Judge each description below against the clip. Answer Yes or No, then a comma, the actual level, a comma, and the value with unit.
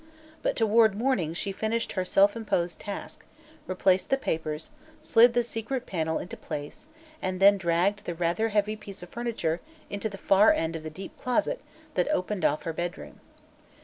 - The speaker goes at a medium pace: Yes, average, 175 wpm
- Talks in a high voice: Yes, high, 195 Hz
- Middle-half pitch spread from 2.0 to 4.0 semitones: No, average, 4.6 semitones